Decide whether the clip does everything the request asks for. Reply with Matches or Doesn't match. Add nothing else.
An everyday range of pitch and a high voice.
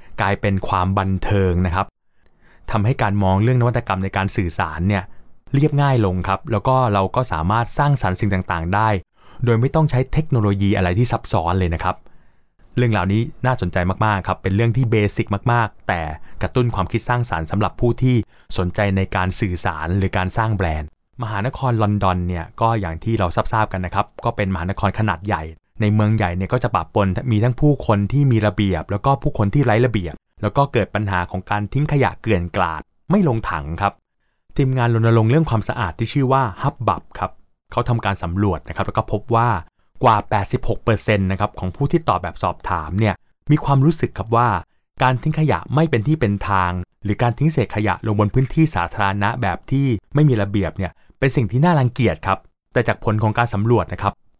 Doesn't match